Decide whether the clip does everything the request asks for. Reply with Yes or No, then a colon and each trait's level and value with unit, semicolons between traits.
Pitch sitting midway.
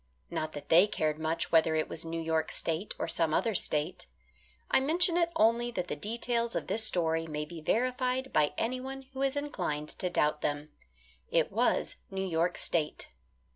Yes: medium, 175 Hz